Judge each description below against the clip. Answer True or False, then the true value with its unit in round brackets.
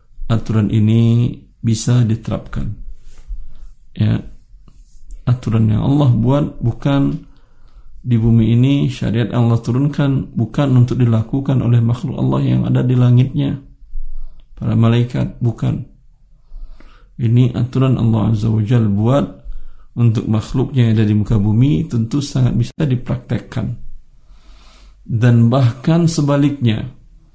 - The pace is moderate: True (110 wpm)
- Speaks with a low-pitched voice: True (120 Hz)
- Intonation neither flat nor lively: True (3.0 semitones)